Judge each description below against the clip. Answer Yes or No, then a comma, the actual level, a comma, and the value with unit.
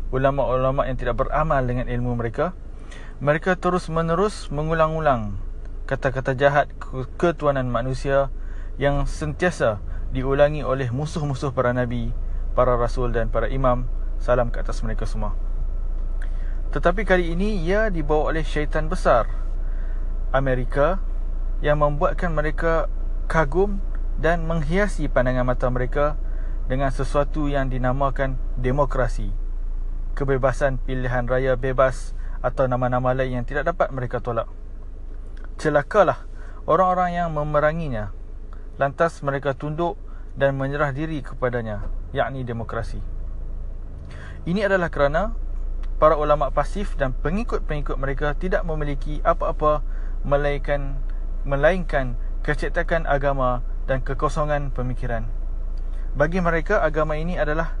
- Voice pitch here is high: No, low, 135 Hz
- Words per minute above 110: No, average, 105 wpm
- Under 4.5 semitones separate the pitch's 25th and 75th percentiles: No, average, 4.9 semitones